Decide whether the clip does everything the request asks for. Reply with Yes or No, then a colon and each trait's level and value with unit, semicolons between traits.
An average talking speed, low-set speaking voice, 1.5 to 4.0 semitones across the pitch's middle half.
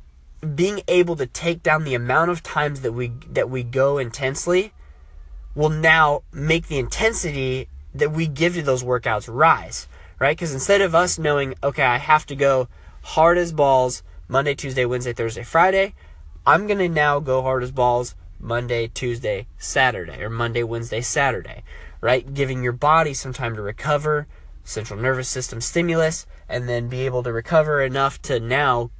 No: average, 170 wpm; low, 130 Hz; average, 4.6 semitones